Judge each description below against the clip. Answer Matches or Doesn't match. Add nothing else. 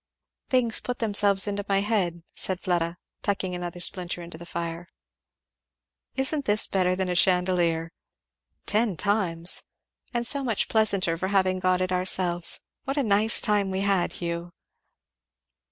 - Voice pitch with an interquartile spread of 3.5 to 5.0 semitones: Doesn't match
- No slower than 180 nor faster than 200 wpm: Doesn't match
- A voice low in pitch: Doesn't match